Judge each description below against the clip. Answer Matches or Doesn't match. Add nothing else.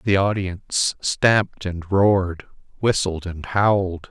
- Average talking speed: Doesn't match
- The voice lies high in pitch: Doesn't match